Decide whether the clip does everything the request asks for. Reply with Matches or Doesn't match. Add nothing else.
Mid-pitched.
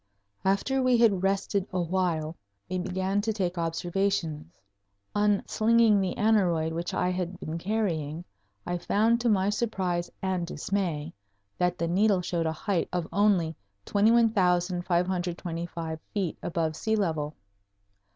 Matches